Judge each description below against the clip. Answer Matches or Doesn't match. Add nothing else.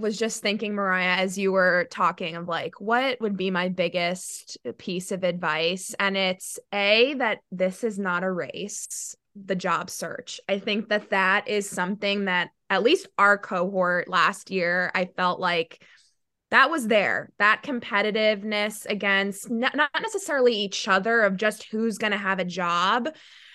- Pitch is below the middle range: Doesn't match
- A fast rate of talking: Doesn't match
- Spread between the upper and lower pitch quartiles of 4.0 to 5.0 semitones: Doesn't match